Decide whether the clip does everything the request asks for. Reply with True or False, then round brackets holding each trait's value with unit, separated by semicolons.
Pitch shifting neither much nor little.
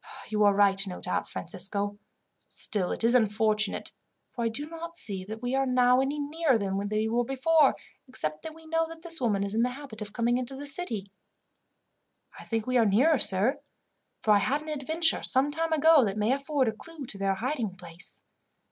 False (6.0 semitones)